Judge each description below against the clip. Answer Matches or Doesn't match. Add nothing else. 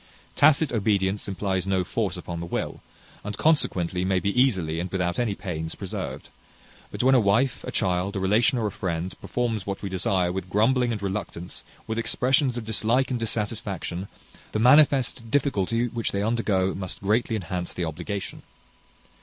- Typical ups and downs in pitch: Matches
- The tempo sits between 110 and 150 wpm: Doesn't match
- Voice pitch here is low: Matches